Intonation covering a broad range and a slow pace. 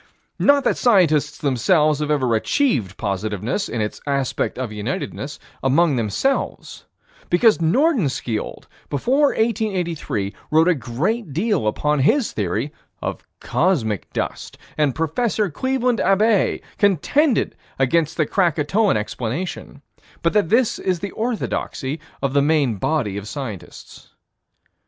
Yes: wide, 8.2 semitones; slow, 120 wpm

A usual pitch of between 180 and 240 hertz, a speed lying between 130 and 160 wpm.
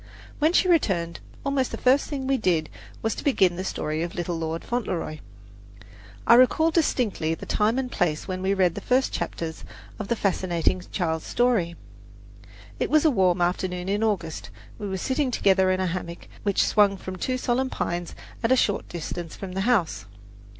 No: high, 190 Hz; average, 185 wpm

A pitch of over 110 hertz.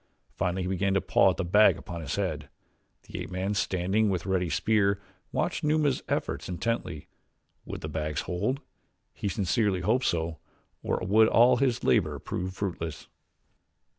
No: very low, 95 Hz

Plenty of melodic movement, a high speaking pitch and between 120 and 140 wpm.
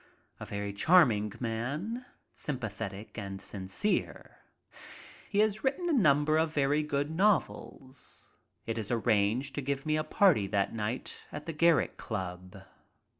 No: wide, 7.2 semitones; low, 135 Hz; slow, 135 wpm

